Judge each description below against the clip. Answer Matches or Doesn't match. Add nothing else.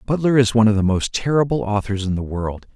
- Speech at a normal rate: Doesn't match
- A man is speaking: Matches